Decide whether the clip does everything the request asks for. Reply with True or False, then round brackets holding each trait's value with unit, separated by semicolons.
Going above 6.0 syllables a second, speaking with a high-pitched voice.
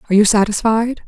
True (7.0 syllables/s; 215 Hz)